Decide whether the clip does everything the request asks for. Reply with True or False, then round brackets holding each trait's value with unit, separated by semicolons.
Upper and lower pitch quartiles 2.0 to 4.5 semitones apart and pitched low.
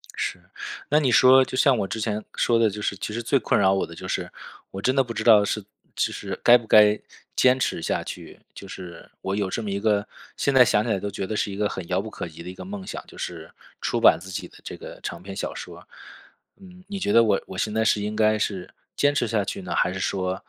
True (3.7 semitones; 105 Hz)